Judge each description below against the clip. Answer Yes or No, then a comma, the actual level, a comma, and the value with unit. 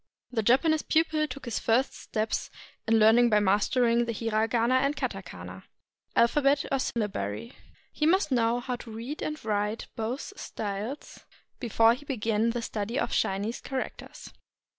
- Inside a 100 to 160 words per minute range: Yes, average, 150 wpm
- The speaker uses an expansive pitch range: No, average, 3.5 semitones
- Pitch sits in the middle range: No, high, 235 Hz